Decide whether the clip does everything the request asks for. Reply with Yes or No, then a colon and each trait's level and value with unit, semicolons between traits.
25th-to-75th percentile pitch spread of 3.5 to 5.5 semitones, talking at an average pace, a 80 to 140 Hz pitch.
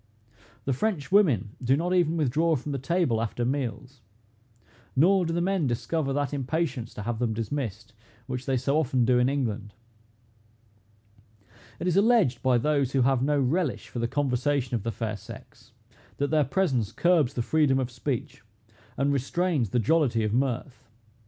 Yes: average, 4.5 semitones; average, 170 wpm; low, 135 Hz